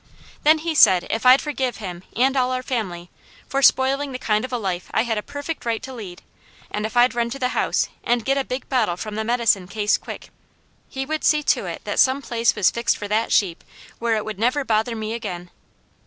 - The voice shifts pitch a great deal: No, average, 3.8 semitones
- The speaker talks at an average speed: No, fast, 230 wpm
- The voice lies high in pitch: Yes, high, 235 Hz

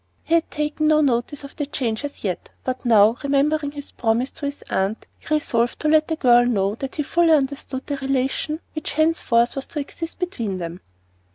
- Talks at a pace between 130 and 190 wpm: No, average, 200 wpm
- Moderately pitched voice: No, very high, 275 Hz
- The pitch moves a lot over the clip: No, average, 4.3 semitones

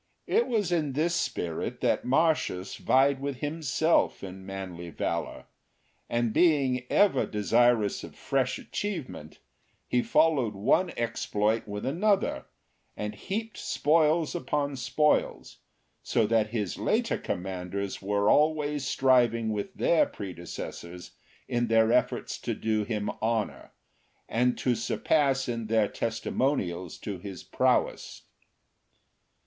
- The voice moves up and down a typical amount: No, wide, 6.2 semitones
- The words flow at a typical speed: No, slow, 120 wpm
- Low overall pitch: Yes, low, 120 Hz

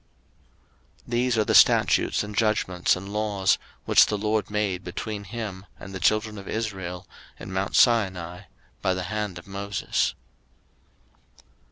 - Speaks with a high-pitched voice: No, low, 100 Hz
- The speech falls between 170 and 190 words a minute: No, average, 145 wpm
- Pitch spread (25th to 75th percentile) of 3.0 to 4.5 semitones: No, narrow, 2.4 semitones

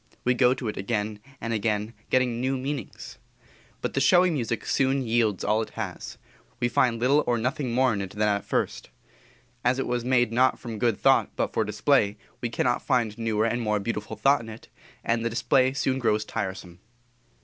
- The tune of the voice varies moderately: Yes, average, 3.1 semitones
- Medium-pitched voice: No, low, 120 Hz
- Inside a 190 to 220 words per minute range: Yes, average, 195 wpm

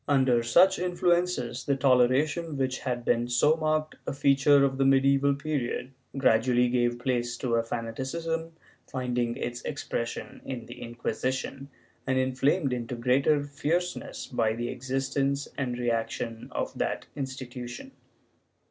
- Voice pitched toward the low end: Yes, low, 130 Hz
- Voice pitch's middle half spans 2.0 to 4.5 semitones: Yes, average, 2.8 semitones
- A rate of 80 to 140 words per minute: Yes, slow, 135 wpm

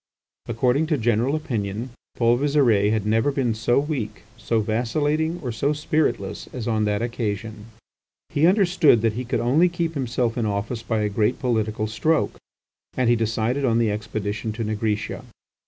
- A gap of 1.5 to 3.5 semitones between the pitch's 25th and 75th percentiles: No, average, 4.4 semitones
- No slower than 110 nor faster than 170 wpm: Yes, average, 165 wpm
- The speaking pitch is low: Yes, low, 115 Hz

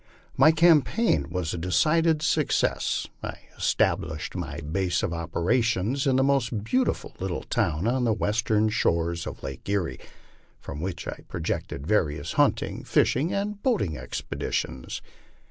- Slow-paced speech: No, average, 145 wpm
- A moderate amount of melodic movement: No, wide, 8.7 semitones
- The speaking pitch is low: Yes, low, 105 Hz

